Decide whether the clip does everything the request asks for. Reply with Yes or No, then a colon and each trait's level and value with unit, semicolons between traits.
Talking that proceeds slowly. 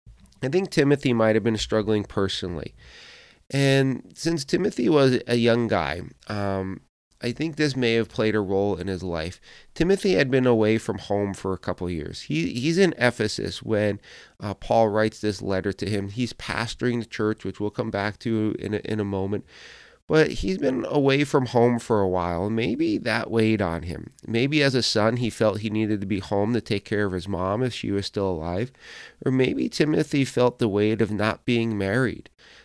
No: average, 200 wpm